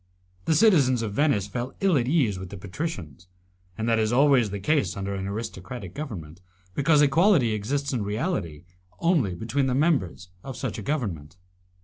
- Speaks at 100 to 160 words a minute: No, average, 170 wpm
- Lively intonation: Yes, wide, 6.6 semitones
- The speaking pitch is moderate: No, low, 115 Hz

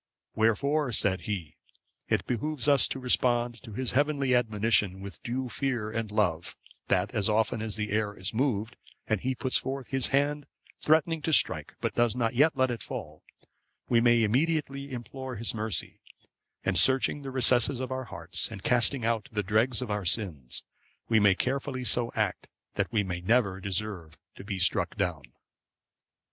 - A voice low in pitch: Yes, low, 115 Hz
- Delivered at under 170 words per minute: No, average, 175 wpm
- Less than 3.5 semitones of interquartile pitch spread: No, average, 4.1 semitones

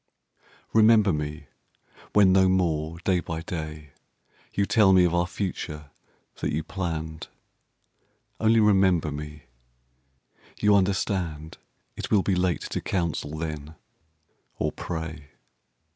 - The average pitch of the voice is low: Yes, very low, 85 Hz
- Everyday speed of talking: No, slow, 115 wpm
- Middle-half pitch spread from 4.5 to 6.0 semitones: No, average, 3.6 semitones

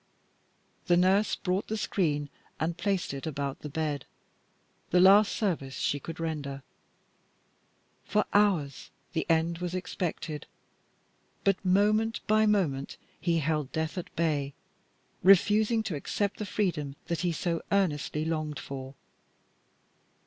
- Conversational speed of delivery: No, slow, 125 wpm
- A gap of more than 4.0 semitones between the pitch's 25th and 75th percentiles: Yes, average, 4.9 semitones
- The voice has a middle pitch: Yes, medium, 170 Hz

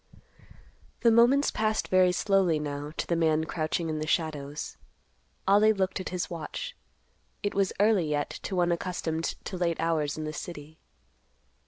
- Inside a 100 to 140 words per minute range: No, average, 160 wpm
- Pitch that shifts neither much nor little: Yes, average, 3.9 semitones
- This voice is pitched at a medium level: Yes, medium, 170 Hz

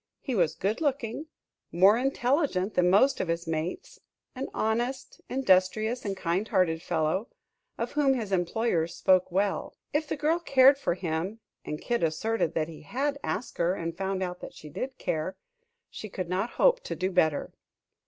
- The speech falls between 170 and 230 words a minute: Yes, average, 175 wpm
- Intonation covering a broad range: Yes, wide, 6.7 semitones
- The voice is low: No, high, 195 Hz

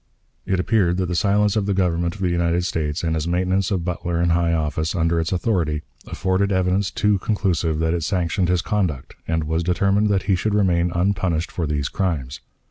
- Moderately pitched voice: No, very low, 90 Hz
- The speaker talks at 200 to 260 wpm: Yes, fast, 205 wpm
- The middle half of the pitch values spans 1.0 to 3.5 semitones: Yes, narrow, 2.6 semitones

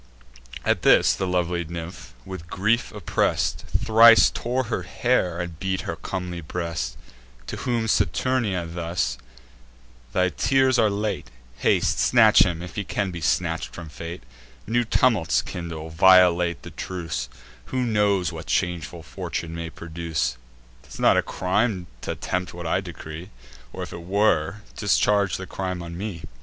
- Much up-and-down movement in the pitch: No, average, 3.6 semitones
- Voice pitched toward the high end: No, very low, 90 Hz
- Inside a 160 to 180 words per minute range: No, average, 150 wpm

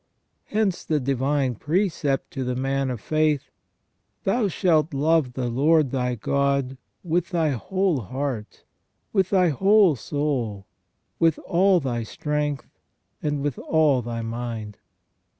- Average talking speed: No, slow, 130 wpm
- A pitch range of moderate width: Yes, average, 4.5 semitones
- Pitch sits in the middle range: Yes, medium, 145 Hz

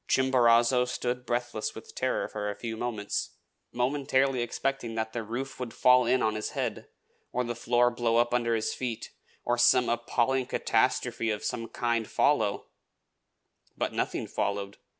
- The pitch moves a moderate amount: No, narrow, 1.6 semitones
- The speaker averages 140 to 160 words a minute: Yes, average, 155 wpm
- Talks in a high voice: No, low, 120 Hz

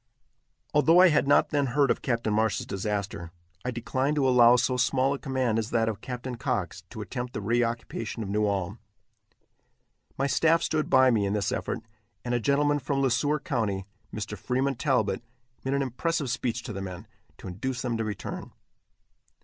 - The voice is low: Yes, low, 125 Hz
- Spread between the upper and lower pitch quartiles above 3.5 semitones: Yes, average, 4.0 semitones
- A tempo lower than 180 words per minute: No, average, 185 wpm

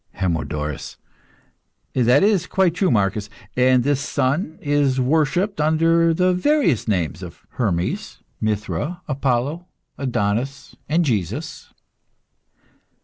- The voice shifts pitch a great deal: Yes, wide, 7.5 semitones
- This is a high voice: No, low, 135 Hz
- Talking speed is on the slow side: Yes, slow, 100 wpm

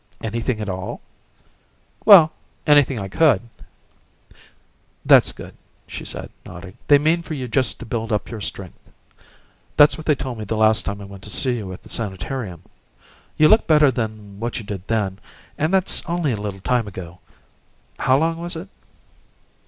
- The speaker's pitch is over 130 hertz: No, low, 115 Hz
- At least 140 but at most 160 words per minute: No, average, 175 wpm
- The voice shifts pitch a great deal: Yes, wide, 6.6 semitones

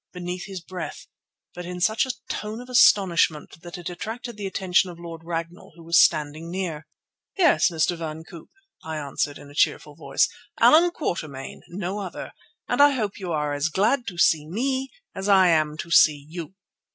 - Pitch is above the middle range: No, medium, 175 Hz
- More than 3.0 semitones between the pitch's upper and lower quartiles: Yes, average, 3.8 semitones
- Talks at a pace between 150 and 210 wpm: Yes, average, 185 wpm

